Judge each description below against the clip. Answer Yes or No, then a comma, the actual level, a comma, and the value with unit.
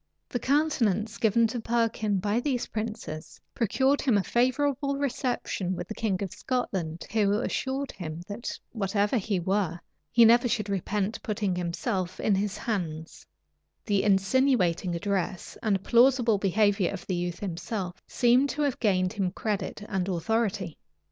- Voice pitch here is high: Yes, high, 210 Hz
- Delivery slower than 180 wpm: Yes, average, 150 wpm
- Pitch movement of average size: Yes, average, 4.1 semitones